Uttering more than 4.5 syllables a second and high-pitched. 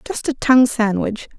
Yes: 5.0 syllables/s; high, 245 Hz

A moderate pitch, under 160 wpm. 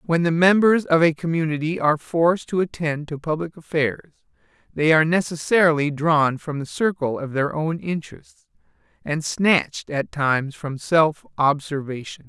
Yes: medium, 160 Hz; average, 150 wpm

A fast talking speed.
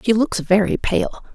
No: average, 180 wpm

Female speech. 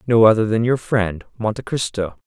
No: male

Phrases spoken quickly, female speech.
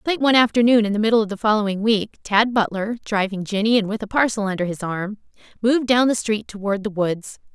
Yes: fast, 225 wpm; female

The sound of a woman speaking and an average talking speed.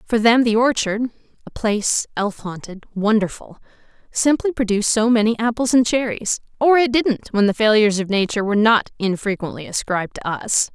Yes: female; average, 170 wpm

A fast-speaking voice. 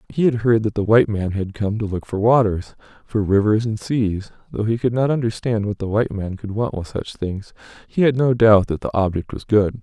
Yes: fast, 245 wpm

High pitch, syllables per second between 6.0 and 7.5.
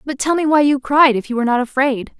Yes: very high, 265 Hz; 6.3 syllables/s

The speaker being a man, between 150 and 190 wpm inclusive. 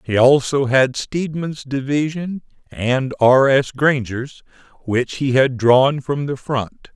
No: male; average, 140 wpm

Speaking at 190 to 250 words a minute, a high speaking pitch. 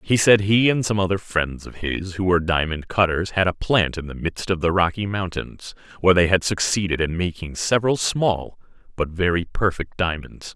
No: average, 200 wpm; very low, 90 Hz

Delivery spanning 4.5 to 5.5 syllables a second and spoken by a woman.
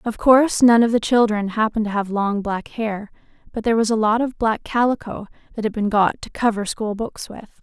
Yes: 5.4 syllables/s; female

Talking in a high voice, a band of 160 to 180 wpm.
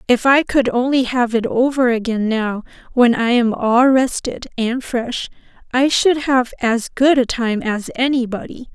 Yes: high, 245 Hz; average, 170 wpm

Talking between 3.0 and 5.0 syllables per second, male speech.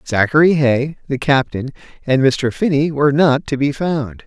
Yes: 4.7 syllables/s; male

